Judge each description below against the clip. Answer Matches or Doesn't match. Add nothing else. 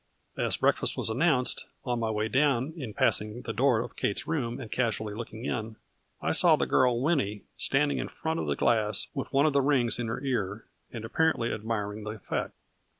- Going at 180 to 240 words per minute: Matches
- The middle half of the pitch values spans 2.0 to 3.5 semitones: Doesn't match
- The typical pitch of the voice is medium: Doesn't match